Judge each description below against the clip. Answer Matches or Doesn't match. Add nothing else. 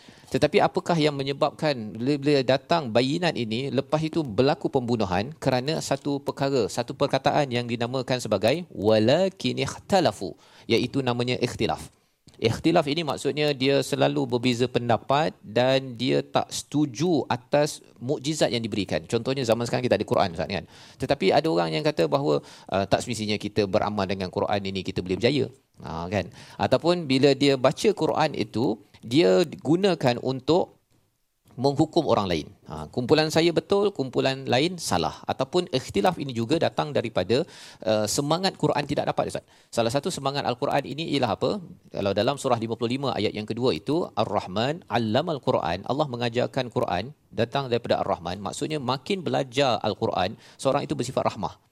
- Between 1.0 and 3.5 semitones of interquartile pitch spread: Doesn't match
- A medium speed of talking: Doesn't match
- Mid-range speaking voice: Doesn't match